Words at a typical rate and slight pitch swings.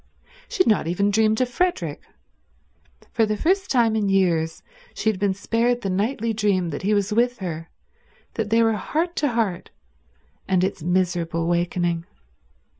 No: average, 165 wpm; average, 4.4 semitones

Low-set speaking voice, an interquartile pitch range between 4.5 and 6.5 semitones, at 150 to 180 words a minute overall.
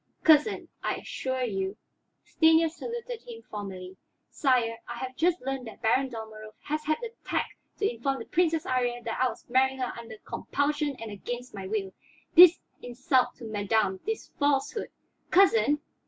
No: very high, 255 Hz; wide, 5.5 semitones; average, 170 wpm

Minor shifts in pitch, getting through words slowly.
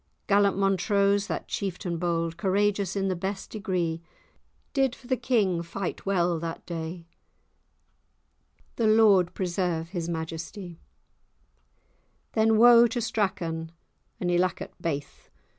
No: average, 3.4 semitones; slow, 115 wpm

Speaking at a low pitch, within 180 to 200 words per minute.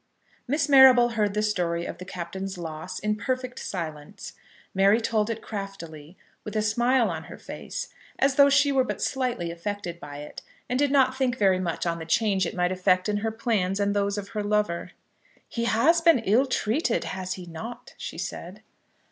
No: high, 210 Hz; average, 190 wpm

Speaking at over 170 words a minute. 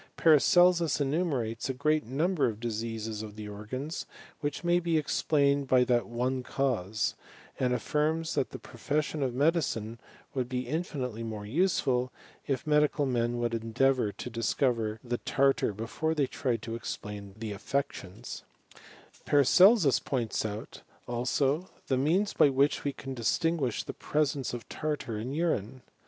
No: average, 145 wpm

